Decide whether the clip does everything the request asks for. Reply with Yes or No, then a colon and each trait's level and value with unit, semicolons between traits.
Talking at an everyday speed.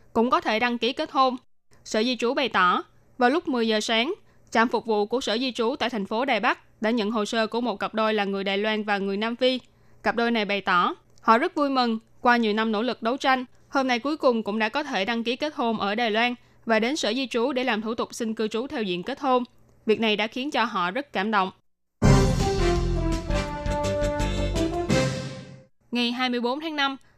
Yes: average, 230 wpm